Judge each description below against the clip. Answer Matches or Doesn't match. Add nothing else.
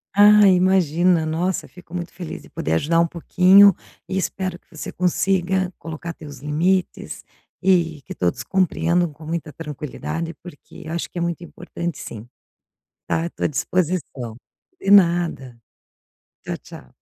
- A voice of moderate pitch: Matches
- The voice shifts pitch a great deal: Doesn't match